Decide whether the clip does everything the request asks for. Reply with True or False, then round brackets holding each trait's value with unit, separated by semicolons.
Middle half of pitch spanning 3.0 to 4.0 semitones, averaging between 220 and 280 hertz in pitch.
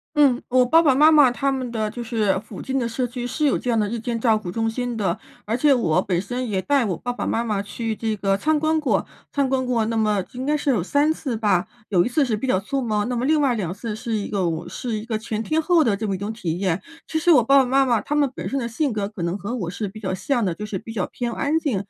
False (4.4 semitones; 230 Hz)